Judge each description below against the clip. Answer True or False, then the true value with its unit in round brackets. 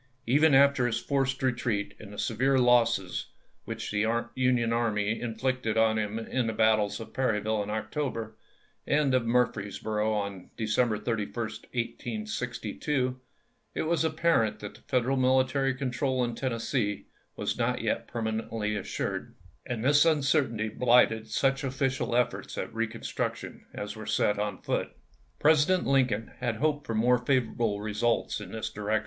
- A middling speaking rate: True (150 wpm)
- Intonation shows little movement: False (3.3 semitones)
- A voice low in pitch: True (120 Hz)